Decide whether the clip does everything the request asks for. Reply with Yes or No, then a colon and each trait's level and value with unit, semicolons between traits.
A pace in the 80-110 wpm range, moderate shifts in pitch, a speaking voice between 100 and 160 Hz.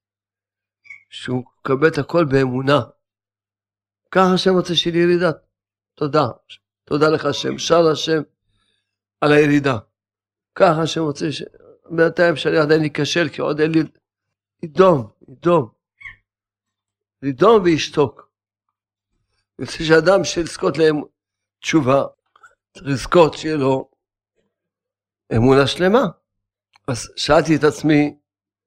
No: average, 105 wpm; wide, 7.9 semitones; medium, 140 Hz